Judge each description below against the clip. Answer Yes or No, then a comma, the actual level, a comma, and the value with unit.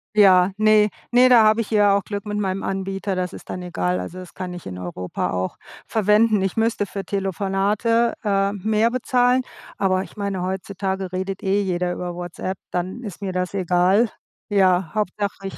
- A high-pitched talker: Yes, high, 195 Hz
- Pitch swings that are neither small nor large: No, narrow, 2.3 semitones